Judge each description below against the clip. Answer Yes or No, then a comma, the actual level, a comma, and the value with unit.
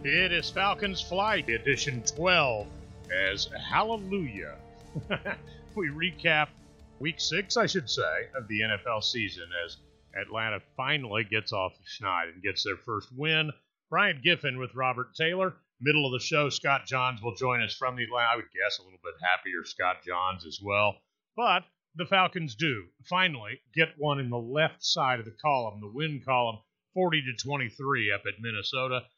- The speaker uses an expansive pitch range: Yes, wide, 5.9 semitones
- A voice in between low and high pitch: No, low, 130 Hz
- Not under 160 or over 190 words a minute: Yes, average, 165 wpm